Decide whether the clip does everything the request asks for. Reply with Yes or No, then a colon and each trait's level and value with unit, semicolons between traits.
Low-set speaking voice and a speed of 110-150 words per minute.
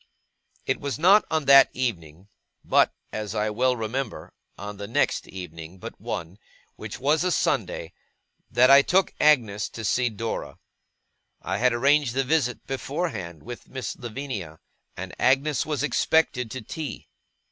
Yes: low, 125 Hz; average, 145 wpm